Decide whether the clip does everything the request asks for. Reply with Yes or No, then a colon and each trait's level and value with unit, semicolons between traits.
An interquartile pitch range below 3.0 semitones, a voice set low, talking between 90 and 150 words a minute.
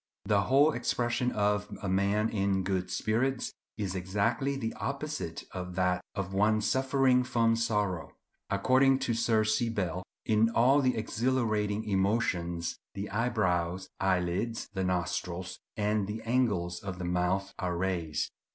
No: average, 4.1 semitones; low, 105 Hz; average, 140 wpm